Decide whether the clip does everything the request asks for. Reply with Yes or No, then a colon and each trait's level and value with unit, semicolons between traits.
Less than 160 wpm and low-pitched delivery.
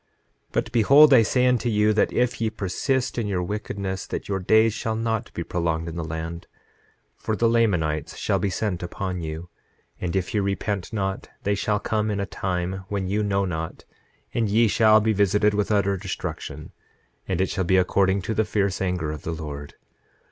No: average, 200 wpm; low, 100 Hz